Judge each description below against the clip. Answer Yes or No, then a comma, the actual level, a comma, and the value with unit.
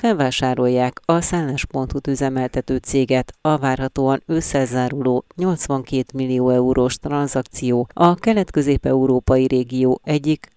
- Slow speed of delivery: Yes, slow, 90 wpm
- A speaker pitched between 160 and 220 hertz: No, low, 130 Hz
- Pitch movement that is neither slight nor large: No, narrow, 2.2 semitones